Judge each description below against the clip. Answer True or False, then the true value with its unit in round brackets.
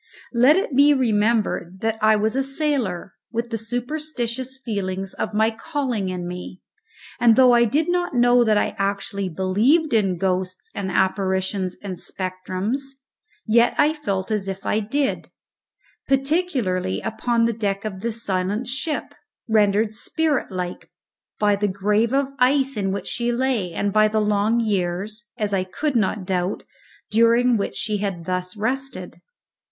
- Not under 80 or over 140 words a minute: False (155 wpm)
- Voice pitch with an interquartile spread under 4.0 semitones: False (4.4 semitones)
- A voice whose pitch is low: False (215 Hz)